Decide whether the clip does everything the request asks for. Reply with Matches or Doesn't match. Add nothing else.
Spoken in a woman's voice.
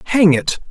Doesn't match